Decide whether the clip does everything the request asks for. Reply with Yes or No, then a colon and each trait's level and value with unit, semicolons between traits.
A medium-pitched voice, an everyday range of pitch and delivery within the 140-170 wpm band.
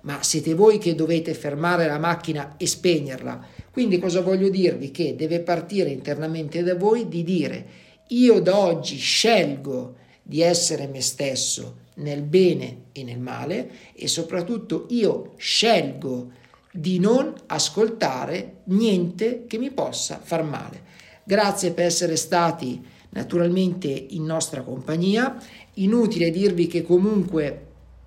No: medium, 170 Hz; average, 4.8 semitones; average, 130 wpm